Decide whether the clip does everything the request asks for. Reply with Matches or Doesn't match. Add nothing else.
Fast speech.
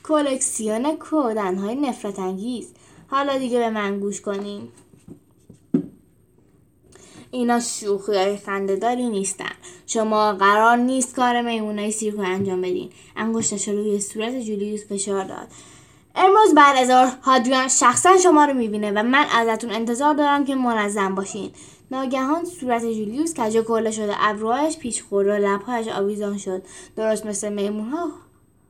Doesn't match